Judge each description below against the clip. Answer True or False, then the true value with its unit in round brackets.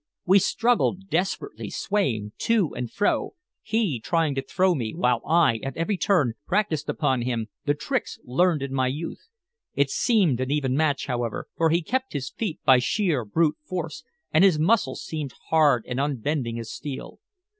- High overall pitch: False (150 Hz)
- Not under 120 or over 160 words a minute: False (170 wpm)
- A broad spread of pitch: True (6.1 semitones)